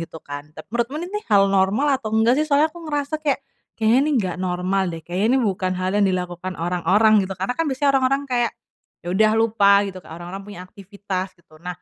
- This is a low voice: No, high, 200 Hz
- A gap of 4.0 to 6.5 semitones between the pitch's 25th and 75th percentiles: Yes, average, 5.0 semitones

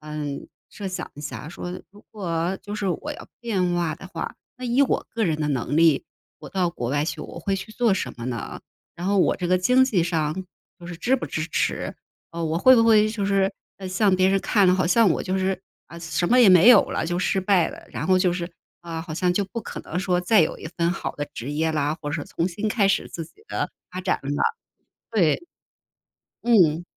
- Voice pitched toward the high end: No, medium, 180 Hz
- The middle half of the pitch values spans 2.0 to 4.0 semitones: Yes, average, 3.7 semitones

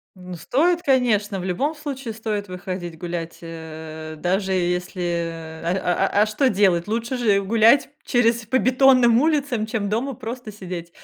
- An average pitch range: No, wide, 5.7 semitones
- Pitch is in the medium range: No, high, 205 Hz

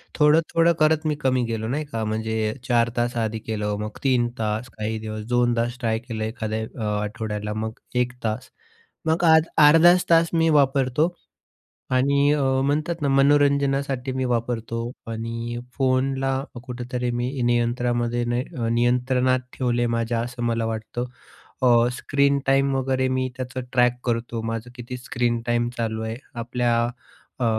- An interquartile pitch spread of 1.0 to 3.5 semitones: Yes, average, 2.8 semitones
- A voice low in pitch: Yes, low, 120 Hz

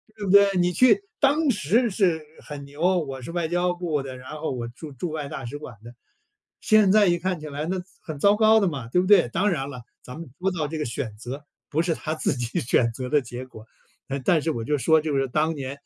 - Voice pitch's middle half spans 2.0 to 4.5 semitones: No, average, 5.2 semitones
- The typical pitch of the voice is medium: Yes, medium, 155 Hz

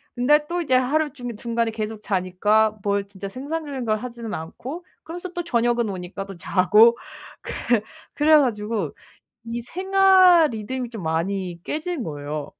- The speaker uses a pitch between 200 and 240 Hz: Yes, high, 235 Hz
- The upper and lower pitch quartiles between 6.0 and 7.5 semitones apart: Yes, wide, 6.7 semitones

